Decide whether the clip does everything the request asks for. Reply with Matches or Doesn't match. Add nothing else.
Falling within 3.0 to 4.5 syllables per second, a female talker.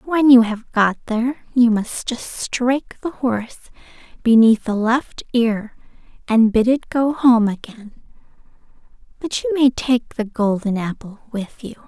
Matches